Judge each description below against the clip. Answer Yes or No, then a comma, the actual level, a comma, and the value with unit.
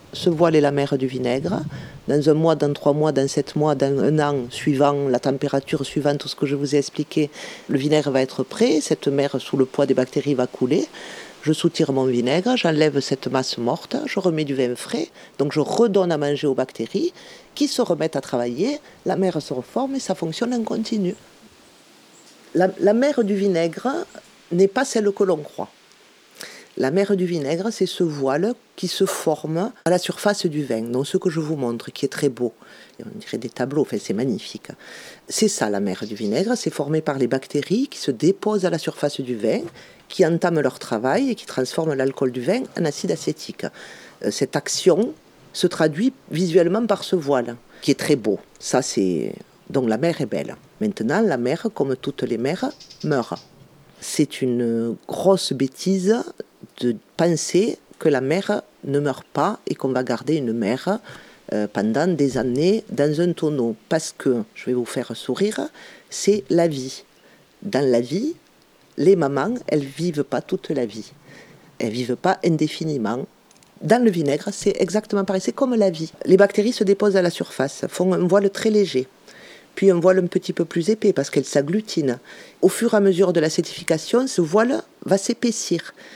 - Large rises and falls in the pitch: Yes, wide, 6.1 semitones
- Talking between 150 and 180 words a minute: No, average, 190 wpm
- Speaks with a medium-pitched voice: Yes, medium, 165 Hz